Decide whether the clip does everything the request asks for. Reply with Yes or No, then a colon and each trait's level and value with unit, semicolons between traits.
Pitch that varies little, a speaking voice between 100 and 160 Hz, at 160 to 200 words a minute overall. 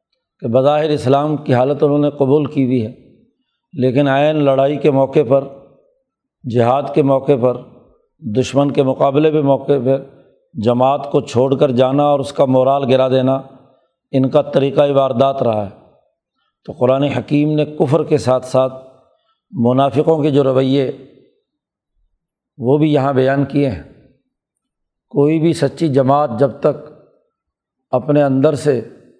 No: narrow, 2.1 semitones; medium, 140 Hz; average, 145 wpm